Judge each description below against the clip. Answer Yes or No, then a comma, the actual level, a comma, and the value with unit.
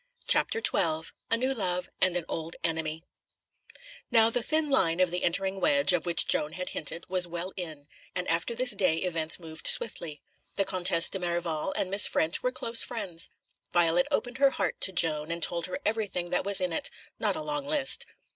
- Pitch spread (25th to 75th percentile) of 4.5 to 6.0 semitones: Yes, average, 5.1 semitones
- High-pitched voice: No, medium, 180 Hz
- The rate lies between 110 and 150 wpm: No, average, 195 wpm